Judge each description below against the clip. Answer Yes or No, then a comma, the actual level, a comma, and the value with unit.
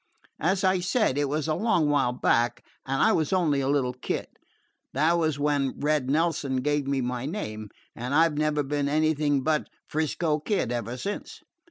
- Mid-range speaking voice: Yes, medium, 145 Hz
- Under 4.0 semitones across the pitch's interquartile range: Yes, average, 2.9 semitones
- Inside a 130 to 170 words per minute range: No, average, 185 wpm